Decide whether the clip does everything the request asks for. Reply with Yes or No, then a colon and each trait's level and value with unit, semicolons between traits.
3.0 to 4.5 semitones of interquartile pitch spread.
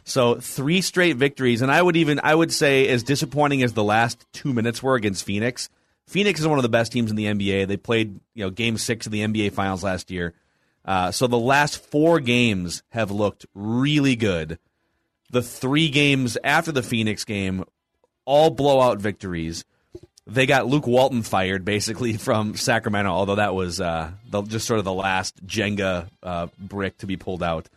No: average, 5.3 semitones